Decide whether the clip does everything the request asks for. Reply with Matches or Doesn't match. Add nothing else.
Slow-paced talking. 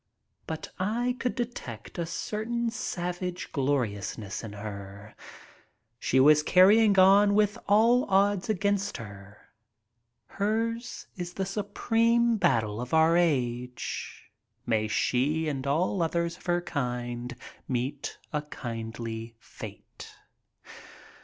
Matches